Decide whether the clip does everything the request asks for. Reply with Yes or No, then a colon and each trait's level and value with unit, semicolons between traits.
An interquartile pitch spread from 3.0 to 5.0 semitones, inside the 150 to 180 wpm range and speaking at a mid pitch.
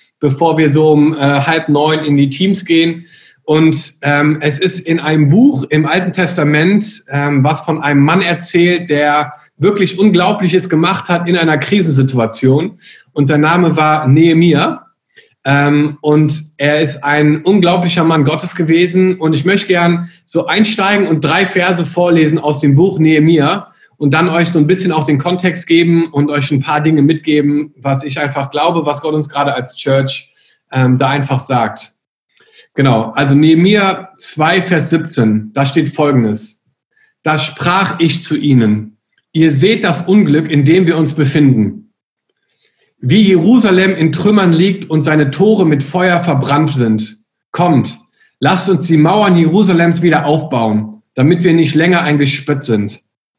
Yes: average, 3.4 semitones; average, 160 wpm; medium, 155 Hz